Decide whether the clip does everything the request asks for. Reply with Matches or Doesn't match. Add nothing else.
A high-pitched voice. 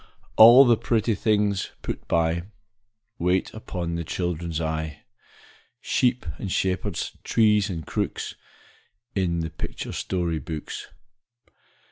Doesn't match